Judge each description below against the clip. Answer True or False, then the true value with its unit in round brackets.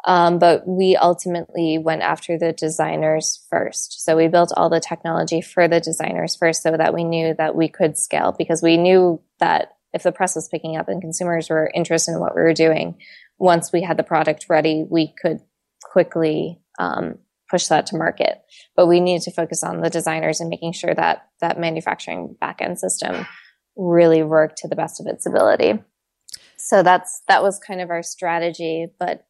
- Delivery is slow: False (190 wpm)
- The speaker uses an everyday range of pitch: False (1.3 semitones)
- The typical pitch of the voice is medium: True (165 Hz)